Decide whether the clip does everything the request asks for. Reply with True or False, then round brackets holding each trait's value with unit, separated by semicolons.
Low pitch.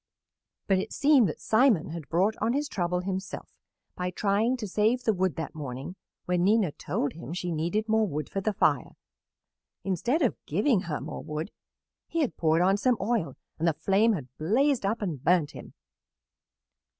False (190 Hz)